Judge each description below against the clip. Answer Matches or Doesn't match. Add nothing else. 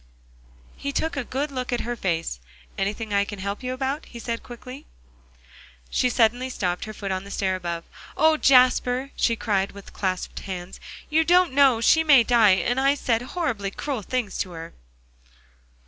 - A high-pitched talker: Matches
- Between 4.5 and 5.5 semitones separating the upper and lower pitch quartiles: Matches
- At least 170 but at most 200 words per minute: Matches